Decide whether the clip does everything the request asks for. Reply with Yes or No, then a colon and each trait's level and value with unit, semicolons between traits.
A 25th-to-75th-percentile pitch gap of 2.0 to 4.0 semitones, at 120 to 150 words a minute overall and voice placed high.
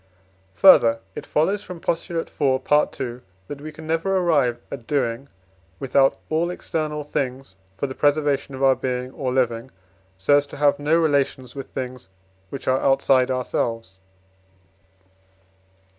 No: average, 2.9 semitones; average, 145 wpm; medium, 140 Hz